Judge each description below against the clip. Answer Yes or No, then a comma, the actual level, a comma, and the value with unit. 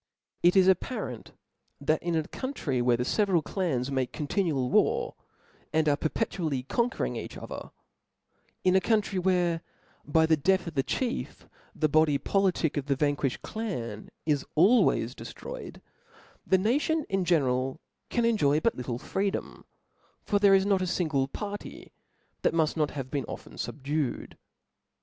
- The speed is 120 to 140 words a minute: No, average, 155 wpm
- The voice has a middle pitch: Yes, medium, 160 Hz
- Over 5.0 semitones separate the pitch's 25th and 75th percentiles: Yes, wide, 5.6 semitones